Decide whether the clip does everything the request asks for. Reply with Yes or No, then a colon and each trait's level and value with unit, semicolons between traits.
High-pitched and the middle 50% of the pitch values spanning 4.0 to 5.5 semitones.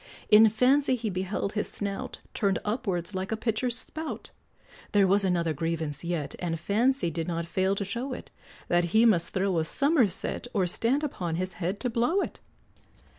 Yes: high, 200 Hz; average, 5.1 semitones